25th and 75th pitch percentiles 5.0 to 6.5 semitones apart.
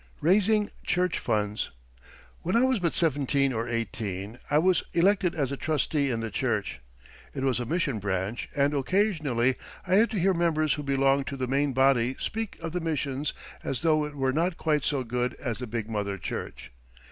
Yes: wide, 5.5 semitones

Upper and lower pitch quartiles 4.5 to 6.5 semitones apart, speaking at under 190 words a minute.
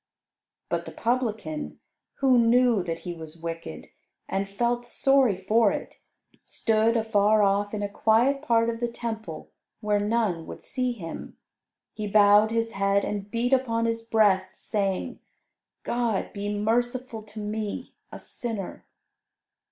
No: average, 2.7 semitones; average, 140 wpm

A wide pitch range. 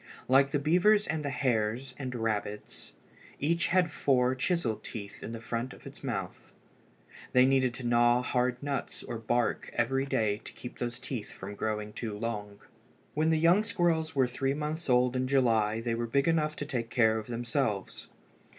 No: average, 3.9 semitones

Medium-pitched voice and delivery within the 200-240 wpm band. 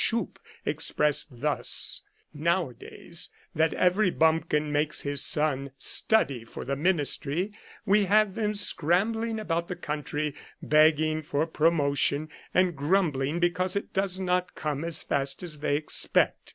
No: medium, 160 Hz; average, 140 wpm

